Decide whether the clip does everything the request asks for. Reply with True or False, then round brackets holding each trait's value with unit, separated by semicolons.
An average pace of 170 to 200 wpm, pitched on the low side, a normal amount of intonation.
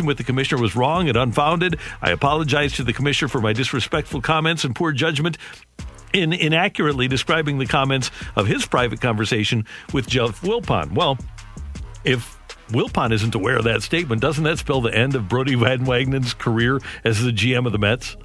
True (180 wpm; 130 Hz; 4.3 semitones)